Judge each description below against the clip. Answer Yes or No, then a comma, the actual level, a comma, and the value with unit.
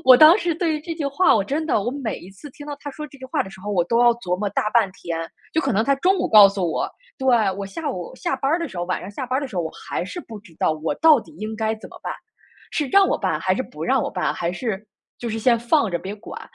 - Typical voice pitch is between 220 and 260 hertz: Yes, high, 235 Hz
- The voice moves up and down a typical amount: No, wide, 6.6 semitones